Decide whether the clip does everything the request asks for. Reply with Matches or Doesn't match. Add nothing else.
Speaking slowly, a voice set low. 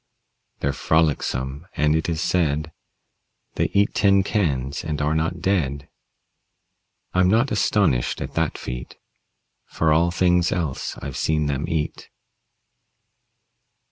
Matches